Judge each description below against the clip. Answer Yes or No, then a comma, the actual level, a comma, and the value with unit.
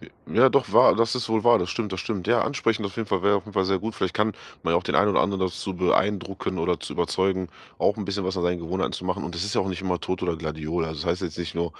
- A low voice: Yes, very low, 95 Hz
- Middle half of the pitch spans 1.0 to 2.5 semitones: No, average, 2.9 semitones